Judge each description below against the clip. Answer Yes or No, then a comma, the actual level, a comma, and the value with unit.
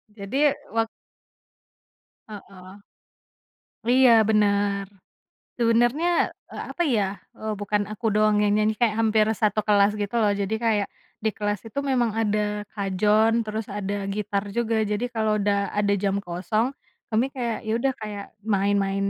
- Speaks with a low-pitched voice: No, high, 210 Hz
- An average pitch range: No, narrow, 1.9 semitones